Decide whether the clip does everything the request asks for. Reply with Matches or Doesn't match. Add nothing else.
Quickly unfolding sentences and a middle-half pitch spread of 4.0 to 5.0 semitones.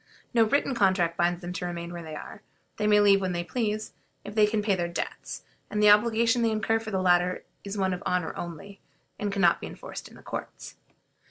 Doesn't match